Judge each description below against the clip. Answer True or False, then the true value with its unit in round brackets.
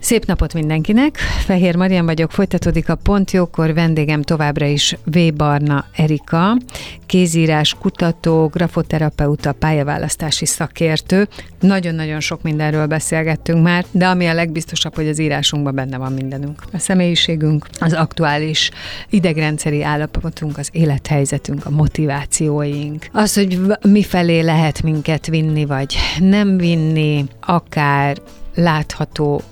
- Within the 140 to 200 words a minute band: False (115 wpm)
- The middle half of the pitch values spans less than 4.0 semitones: True (2.6 semitones)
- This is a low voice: False (160 Hz)